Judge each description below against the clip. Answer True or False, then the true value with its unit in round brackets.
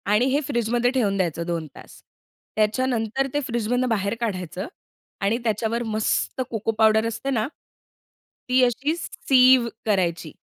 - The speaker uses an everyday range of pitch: True (3.3 semitones)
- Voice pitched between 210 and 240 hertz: True (225 Hz)